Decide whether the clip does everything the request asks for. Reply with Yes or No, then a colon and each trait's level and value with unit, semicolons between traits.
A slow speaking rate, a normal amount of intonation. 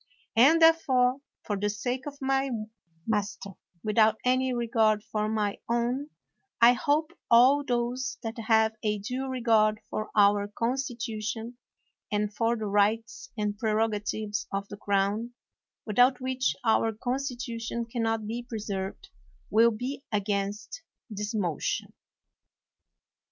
Yes: slow, 130 wpm; average, 3.0 semitones